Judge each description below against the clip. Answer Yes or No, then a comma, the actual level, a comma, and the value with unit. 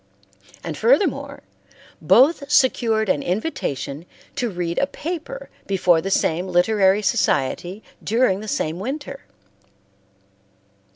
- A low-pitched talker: No, high, 205 Hz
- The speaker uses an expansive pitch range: Yes, wide, 6.9 semitones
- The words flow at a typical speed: No, slow, 105 wpm